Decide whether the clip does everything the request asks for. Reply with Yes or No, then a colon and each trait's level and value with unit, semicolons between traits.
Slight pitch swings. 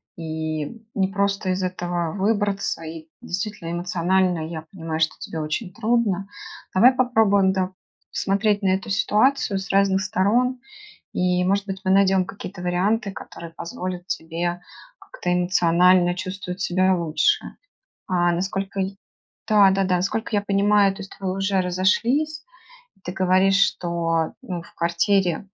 Yes: narrow, 2.2 semitones